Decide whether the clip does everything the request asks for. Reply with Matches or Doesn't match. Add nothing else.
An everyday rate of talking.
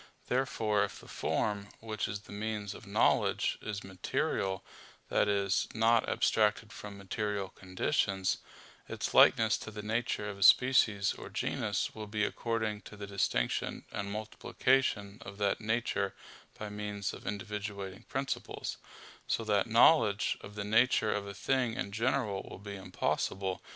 Matches